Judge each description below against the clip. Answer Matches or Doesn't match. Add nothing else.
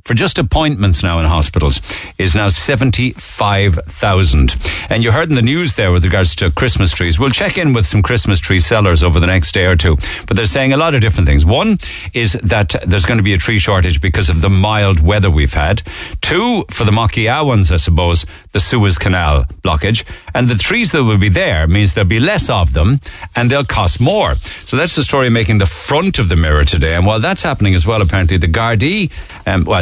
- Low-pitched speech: Matches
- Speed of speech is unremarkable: Doesn't match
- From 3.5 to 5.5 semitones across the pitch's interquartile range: Matches